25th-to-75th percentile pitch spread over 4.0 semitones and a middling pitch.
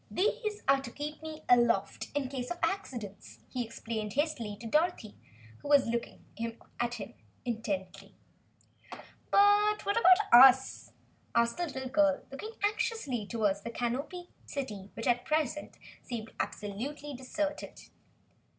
No: average, 5.1 semitones; very high, 260 Hz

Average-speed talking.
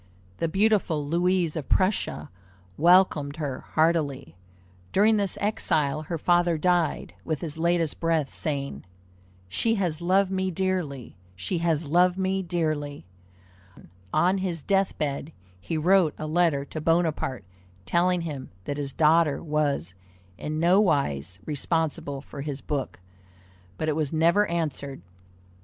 No: slow, 130 wpm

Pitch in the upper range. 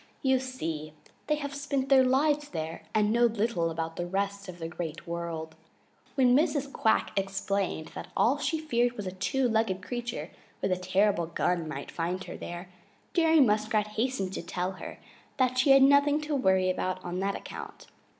Yes: high, 205 Hz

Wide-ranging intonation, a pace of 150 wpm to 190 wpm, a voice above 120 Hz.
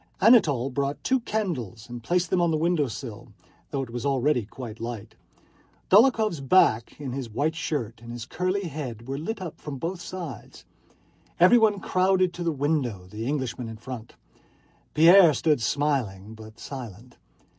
Yes: wide, 6.7 semitones; average, 160 wpm; medium, 140 Hz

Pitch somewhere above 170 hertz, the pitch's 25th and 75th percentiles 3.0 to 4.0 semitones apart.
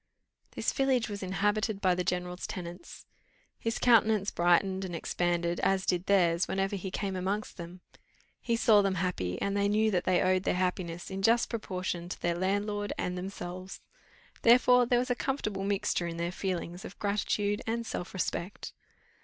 No: high, 190 Hz; narrow, 2.6 semitones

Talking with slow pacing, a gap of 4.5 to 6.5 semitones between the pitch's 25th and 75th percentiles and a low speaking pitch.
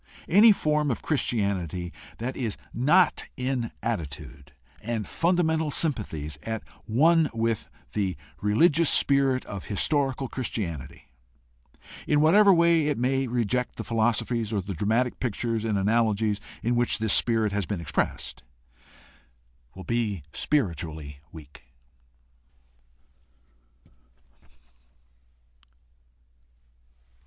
Yes: slow, 105 wpm; wide, 5.6 semitones; low, 115 Hz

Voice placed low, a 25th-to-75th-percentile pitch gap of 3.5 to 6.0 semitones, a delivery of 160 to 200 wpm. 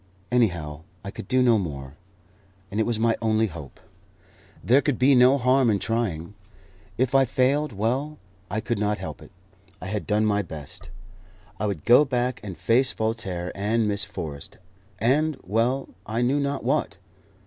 Yes: low, 110 Hz; average, 4.5 semitones; average, 170 wpm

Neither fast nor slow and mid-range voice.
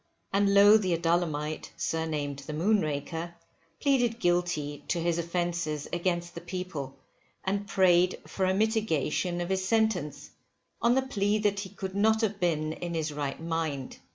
Yes: average, 155 wpm; medium, 175 Hz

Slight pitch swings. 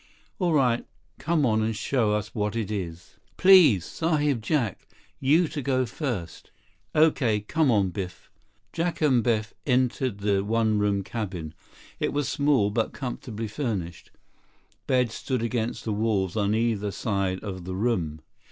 No: average, 4.6 semitones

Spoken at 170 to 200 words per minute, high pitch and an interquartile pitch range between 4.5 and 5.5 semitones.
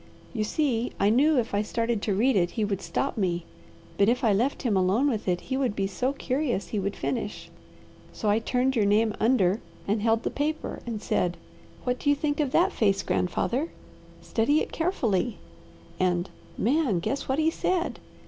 Yes: average, 195 wpm; high, 230 Hz; average, 5.0 semitones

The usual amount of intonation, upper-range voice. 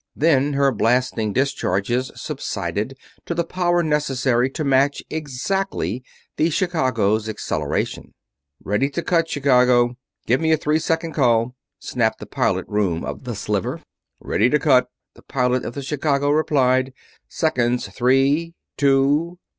No: average, 3.7 semitones; low, 135 Hz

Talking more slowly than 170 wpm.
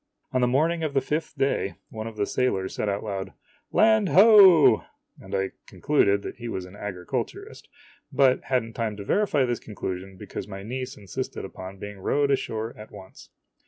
No: average, 185 wpm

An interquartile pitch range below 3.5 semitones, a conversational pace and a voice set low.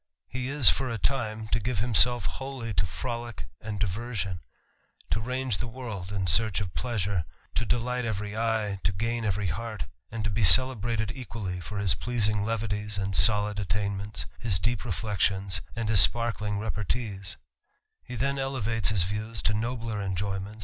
Yes: average, 2.9 semitones; average, 160 wpm; low, 110 Hz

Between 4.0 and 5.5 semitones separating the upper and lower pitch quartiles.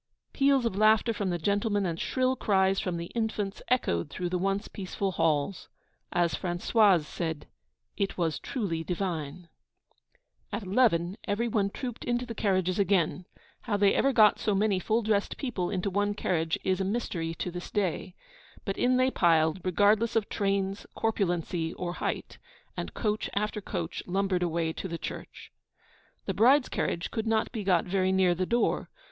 No: average, 3.6 semitones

